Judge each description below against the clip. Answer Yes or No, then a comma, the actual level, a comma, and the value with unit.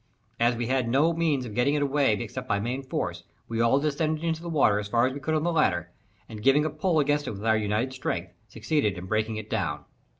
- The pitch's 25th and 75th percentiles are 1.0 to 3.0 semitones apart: No, wide, 5.5 semitones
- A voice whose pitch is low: Yes, low, 130 Hz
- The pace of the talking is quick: Yes, fast, 245 wpm